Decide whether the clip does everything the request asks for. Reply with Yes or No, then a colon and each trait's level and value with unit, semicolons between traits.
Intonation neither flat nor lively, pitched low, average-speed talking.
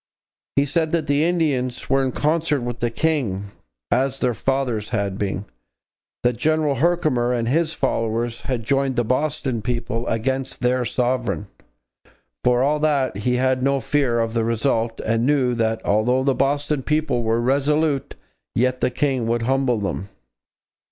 Yes: average, 3.3 semitones; low, 130 Hz; average, 160 wpm